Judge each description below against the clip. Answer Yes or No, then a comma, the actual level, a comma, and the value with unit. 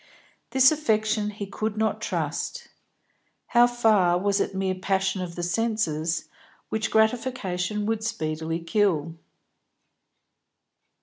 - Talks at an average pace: No, slow, 110 wpm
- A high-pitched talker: Yes, high, 205 Hz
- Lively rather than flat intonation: No, average, 3.8 semitones